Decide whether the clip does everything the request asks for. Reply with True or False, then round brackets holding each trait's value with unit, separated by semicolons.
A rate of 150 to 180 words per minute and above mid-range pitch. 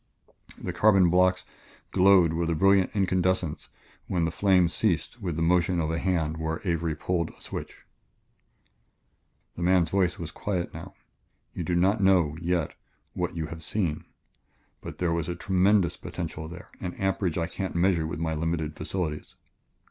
False (165 wpm; 85 Hz)